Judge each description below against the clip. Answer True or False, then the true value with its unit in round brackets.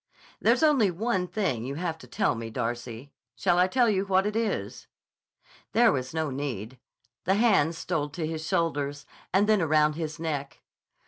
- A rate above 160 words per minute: True (175 wpm)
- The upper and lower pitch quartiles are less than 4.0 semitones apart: False (5.5 semitones)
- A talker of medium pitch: True (160 Hz)